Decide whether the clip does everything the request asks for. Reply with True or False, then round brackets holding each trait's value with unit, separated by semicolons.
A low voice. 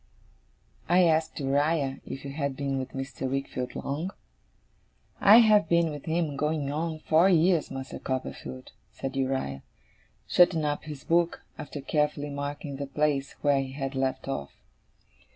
False (145 Hz)